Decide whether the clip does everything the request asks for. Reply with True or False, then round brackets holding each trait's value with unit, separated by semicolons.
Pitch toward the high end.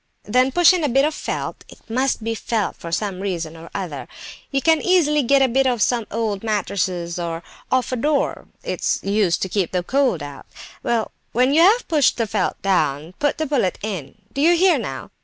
True (225 Hz)